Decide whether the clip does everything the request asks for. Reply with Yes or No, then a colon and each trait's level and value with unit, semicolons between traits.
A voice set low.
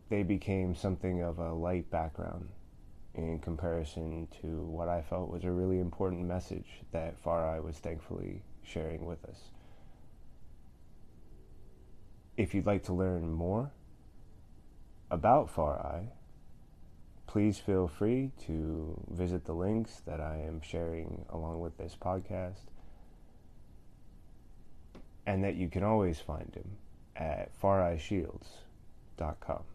Yes: very low, 90 Hz